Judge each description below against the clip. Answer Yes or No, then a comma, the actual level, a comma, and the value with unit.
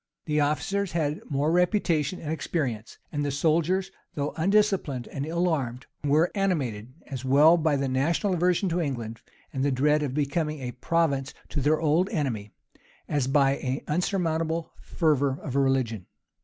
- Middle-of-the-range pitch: Yes, medium, 150 Hz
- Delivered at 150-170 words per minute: Yes, average, 155 wpm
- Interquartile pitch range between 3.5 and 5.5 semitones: Yes, average, 3.8 semitones